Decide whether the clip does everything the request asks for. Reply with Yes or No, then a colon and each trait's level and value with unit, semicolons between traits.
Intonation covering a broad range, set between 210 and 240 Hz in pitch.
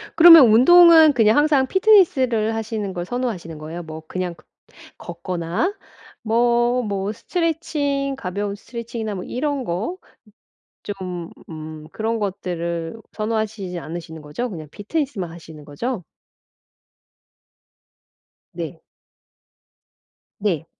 Yes: wide, 6.8 semitones; high, 215 Hz